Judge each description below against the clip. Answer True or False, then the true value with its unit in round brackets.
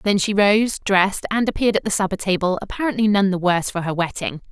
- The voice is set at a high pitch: True (200 Hz)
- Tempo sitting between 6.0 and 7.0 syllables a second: True (6.5 syllables/s)